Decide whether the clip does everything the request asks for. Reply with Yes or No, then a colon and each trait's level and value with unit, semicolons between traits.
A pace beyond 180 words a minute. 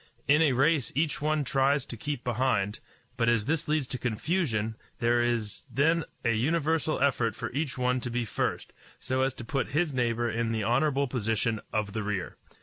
Yes: average, 190 wpm